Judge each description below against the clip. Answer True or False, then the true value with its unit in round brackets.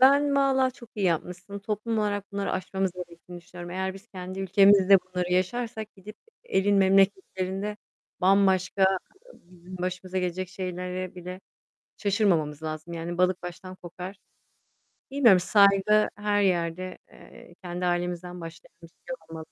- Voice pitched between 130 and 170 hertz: False (185 Hz)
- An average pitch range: False (2.2 semitones)